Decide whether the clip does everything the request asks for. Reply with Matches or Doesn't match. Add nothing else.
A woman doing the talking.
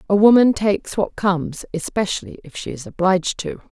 Matches